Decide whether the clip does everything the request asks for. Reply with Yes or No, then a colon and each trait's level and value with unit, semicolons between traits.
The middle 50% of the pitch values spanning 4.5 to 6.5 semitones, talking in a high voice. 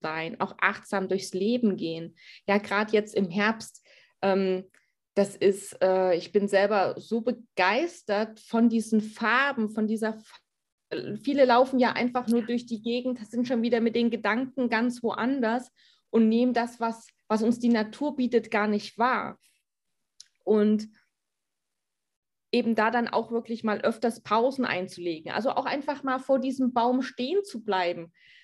No: average, 3.2 semitones; high, 225 Hz